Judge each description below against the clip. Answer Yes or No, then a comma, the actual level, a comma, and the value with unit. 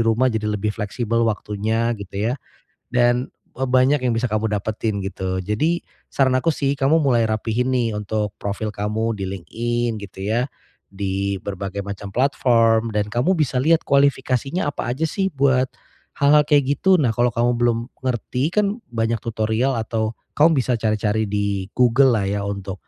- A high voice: No, low, 115 Hz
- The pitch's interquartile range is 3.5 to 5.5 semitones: Yes, average, 3.8 semitones